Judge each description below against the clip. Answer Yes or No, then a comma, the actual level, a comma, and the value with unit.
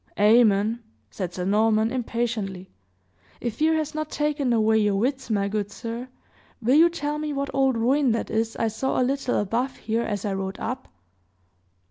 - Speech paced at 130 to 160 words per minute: No, average, 175 wpm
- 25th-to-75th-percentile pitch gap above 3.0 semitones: Yes, average, 4.1 semitones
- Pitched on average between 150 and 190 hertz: No, high, 230 Hz